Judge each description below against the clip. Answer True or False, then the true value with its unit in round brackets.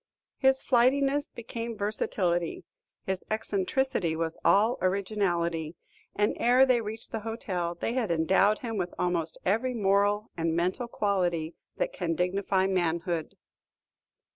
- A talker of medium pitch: False (200 Hz)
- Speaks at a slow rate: True (125 wpm)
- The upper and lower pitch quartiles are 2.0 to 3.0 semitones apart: False (4.8 semitones)